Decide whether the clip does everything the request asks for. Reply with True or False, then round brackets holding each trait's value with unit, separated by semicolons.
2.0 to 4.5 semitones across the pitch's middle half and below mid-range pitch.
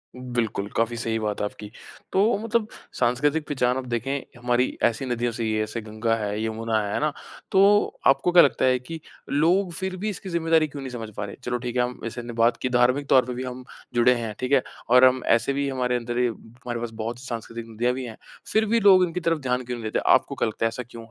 True (3.5 semitones; 125 Hz)